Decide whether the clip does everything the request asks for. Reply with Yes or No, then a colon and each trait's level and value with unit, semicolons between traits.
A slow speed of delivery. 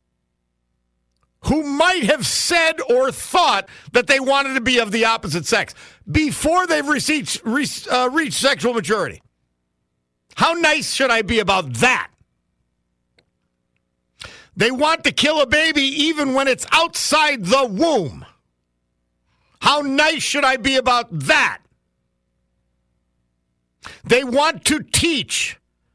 Yes: slow, 125 wpm